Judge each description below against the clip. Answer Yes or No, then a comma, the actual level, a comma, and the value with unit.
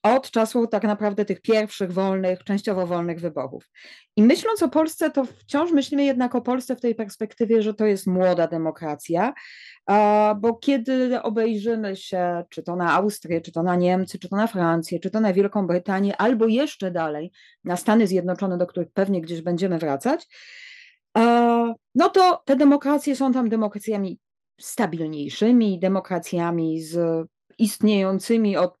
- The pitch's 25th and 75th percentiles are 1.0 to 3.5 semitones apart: No, average, 4.8 semitones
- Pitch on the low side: No, high, 210 Hz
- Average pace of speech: Yes, average, 150 wpm